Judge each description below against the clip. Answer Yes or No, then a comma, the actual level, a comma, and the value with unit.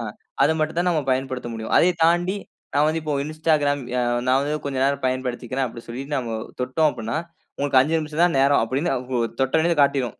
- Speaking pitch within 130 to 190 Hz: Yes, medium, 140 Hz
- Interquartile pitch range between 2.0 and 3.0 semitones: No, average, 3.5 semitones